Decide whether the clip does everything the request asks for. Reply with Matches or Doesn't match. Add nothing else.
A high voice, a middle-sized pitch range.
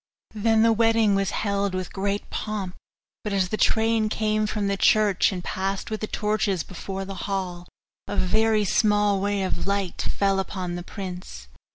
Doesn't match